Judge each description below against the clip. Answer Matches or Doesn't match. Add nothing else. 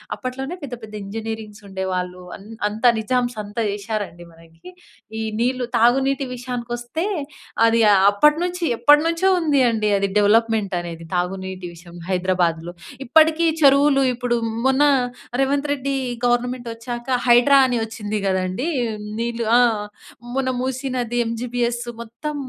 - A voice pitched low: Doesn't match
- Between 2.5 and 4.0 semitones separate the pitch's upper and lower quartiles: Doesn't match